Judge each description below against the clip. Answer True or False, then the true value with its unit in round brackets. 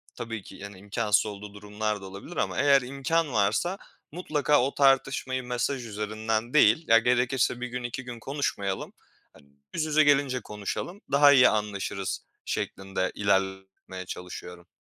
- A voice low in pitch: True (115 Hz)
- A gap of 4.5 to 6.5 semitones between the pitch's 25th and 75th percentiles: True (5.1 semitones)